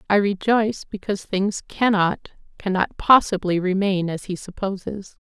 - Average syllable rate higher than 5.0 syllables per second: No, 4.9 syllables/s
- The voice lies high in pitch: Yes, high, 195 Hz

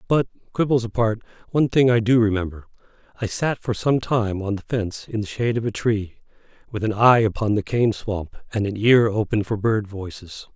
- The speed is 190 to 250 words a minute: Yes, fast, 205 wpm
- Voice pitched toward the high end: No, low, 110 Hz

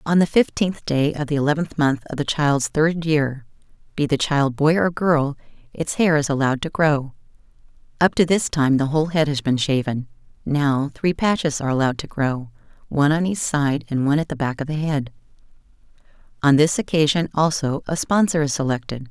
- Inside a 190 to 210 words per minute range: Yes, average, 195 wpm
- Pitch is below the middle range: No, medium, 150 Hz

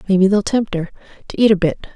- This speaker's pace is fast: Yes, fast, 245 wpm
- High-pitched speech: Yes, high, 195 Hz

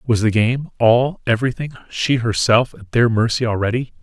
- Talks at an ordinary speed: Yes, average, 165 wpm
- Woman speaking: No, male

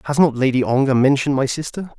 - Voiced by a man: Yes, male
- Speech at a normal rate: No, fast, 210 wpm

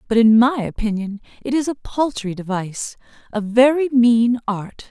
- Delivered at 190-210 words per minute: No, average, 160 wpm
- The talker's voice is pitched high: Yes, high, 230 Hz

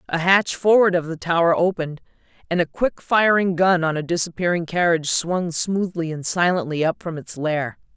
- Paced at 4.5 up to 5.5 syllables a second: Yes, 5.2 syllables/s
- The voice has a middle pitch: Yes, medium, 170 Hz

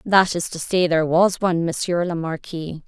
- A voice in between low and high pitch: Yes, medium, 170 Hz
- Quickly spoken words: Yes, fast, 210 wpm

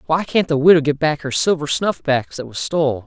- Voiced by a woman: No, male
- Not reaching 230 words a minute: No, fast, 235 wpm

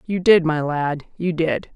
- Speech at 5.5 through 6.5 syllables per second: No, 4.0 syllables/s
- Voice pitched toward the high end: No, medium, 165 Hz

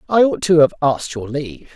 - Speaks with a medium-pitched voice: Yes, medium, 150 Hz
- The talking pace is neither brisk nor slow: No, fast, 240 wpm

